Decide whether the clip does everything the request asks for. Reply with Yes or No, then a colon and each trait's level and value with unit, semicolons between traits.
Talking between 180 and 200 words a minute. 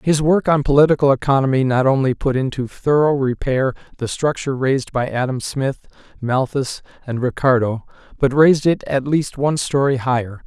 No: average, 160 wpm